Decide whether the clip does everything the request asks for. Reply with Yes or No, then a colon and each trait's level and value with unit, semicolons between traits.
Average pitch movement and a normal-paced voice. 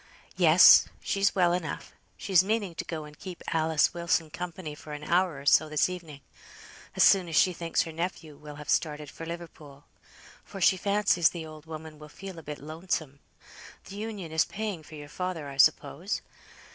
Yes: average, 3.2 semitones; average, 185 wpm